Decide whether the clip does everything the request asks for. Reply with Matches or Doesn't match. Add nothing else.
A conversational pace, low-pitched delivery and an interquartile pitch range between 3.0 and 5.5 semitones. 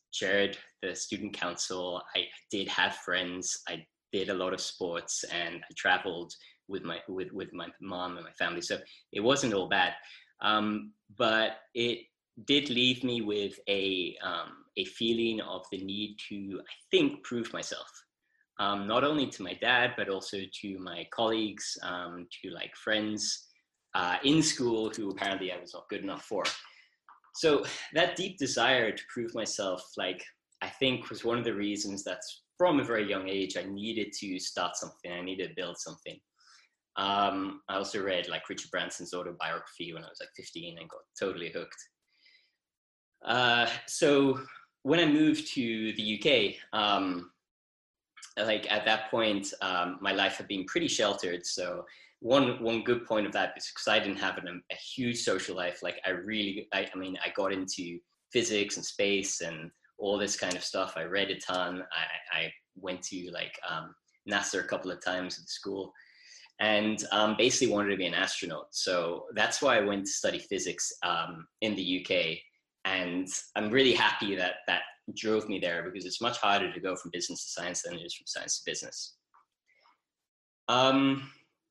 Matches